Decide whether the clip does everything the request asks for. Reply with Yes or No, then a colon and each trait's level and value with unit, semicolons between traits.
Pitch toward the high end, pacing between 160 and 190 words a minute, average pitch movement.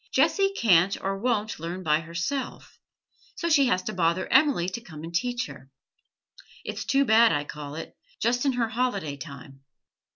No: high, 195 Hz; average, 170 wpm; wide, 7.0 semitones